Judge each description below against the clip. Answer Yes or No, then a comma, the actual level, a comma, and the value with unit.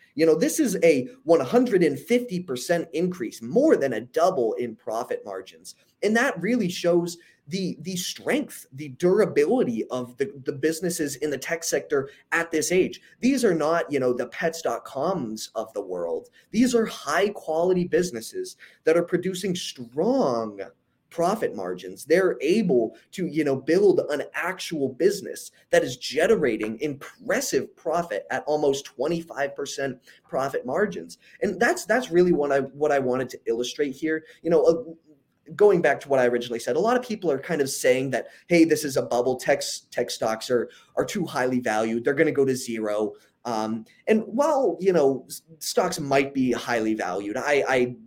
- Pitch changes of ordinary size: No, wide, 6.8 semitones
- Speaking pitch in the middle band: Yes, medium, 160 Hz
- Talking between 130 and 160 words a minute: No, average, 170 wpm